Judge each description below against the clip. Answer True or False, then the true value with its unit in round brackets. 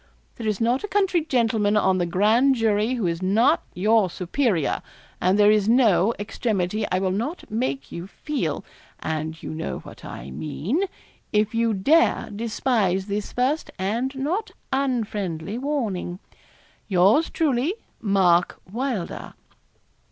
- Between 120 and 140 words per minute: True (135 wpm)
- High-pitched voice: True (215 Hz)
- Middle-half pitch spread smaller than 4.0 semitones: False (5.3 semitones)